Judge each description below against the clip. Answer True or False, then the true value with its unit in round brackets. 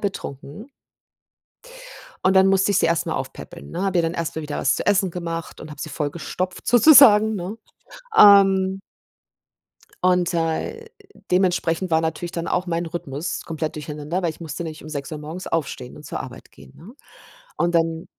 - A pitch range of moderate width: True (3.2 semitones)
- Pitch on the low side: False (170 Hz)